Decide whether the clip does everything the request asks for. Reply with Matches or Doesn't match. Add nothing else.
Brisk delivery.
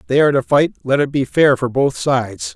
Matches